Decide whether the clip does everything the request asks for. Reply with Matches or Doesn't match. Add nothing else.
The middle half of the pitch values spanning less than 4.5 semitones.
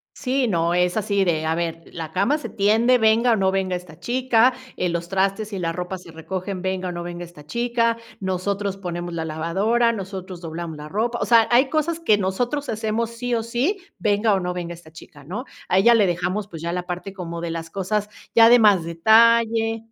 Doesn't match